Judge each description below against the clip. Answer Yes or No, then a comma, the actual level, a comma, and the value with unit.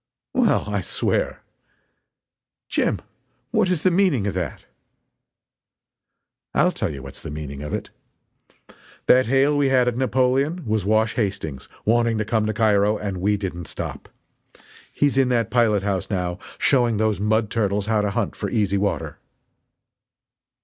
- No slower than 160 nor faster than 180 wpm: No, average, 150 wpm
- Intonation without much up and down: No, average, 4.0 semitones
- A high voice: No, low, 110 Hz